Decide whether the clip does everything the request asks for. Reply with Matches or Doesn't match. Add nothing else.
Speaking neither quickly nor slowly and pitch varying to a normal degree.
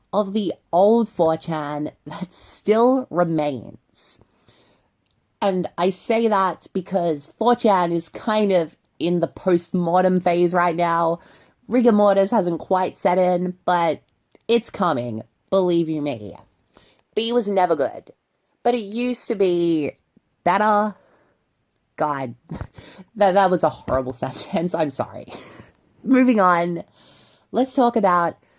Doesn't match